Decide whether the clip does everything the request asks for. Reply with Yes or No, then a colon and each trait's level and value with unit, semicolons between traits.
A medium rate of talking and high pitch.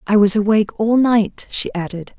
Yes: average, 190 wpm; high, 220 Hz